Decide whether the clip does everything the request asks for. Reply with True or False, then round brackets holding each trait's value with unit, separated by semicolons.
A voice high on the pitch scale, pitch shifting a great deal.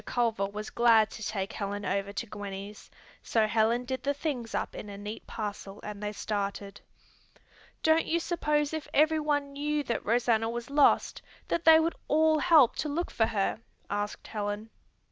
True (225 Hz; 6.1 semitones)